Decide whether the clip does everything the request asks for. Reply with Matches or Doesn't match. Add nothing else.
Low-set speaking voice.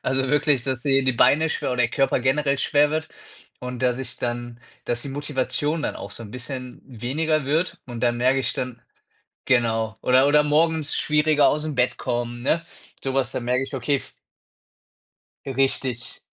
Matches